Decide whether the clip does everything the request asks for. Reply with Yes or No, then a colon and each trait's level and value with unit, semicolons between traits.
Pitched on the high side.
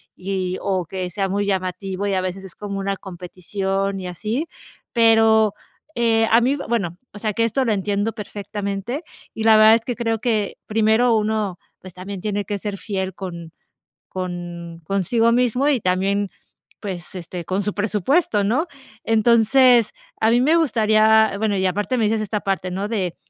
Yes: high, 205 Hz